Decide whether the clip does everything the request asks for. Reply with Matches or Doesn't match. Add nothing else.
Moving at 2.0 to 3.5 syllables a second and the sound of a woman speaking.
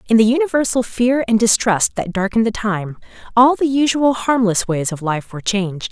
Doesn't match